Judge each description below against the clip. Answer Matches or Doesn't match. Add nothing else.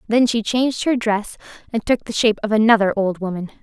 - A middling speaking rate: Doesn't match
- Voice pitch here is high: Matches